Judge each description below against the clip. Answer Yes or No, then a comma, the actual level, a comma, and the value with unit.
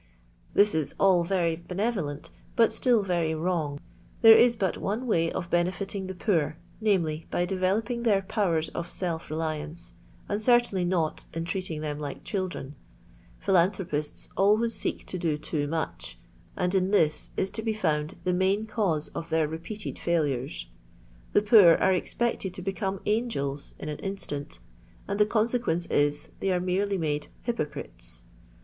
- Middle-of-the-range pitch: Yes, medium, 180 Hz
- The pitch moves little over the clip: No, average, 4.4 semitones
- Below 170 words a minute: Yes, average, 155 wpm